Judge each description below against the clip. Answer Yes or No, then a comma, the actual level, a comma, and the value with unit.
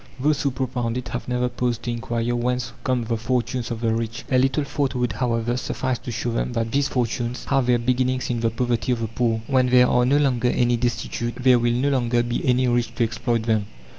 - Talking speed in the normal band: No, fast, 230 wpm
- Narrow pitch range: Yes, narrow, 1.4 semitones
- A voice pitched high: No, low, 120 Hz